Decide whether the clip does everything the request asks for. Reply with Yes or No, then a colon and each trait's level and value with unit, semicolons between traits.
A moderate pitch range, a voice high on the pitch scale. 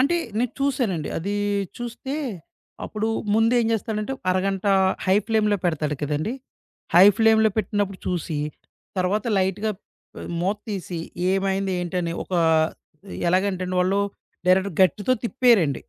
Yes: average, 3.3 semitones; high, 195 Hz